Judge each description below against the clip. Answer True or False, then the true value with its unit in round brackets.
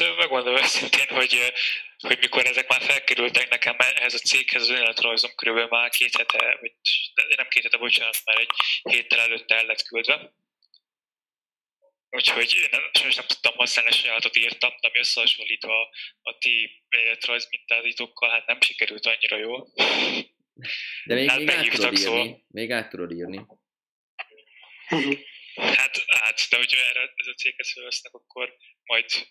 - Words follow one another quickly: False (145 wpm)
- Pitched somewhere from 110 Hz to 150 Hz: True (120 Hz)